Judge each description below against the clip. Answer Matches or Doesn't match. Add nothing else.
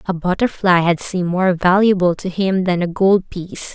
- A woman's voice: Matches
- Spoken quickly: Doesn't match